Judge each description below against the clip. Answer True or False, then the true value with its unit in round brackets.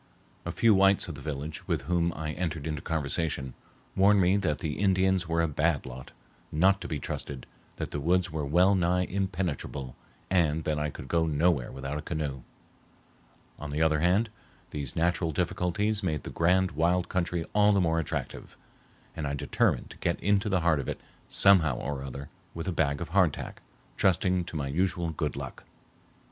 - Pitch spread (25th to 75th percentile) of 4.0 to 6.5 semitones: False (3.6 semitones)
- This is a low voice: True (85 Hz)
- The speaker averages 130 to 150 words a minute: False (185 wpm)